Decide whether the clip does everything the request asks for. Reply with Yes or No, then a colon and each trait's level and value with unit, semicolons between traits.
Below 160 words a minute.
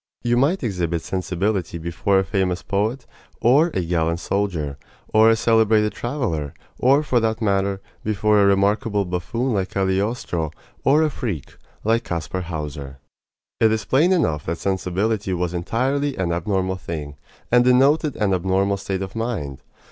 Yes: average, 150 wpm